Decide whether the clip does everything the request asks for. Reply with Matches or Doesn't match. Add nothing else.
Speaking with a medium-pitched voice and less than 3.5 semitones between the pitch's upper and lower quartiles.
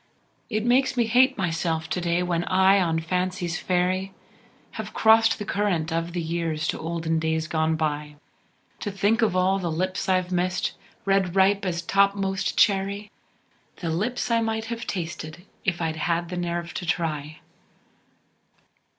Matches